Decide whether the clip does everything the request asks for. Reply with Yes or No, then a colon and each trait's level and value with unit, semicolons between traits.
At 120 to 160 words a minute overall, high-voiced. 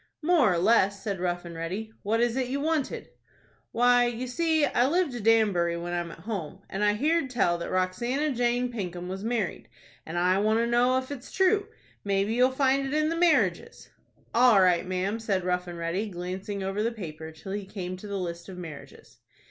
No: fast, 205 wpm; high, 210 Hz